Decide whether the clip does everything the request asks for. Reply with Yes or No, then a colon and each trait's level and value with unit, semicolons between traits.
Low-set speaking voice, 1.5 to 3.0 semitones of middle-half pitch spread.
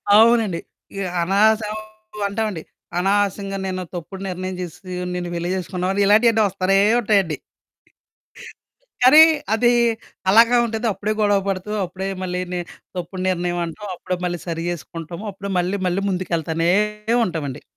No: medium, 185 Hz; average, 2.7 semitones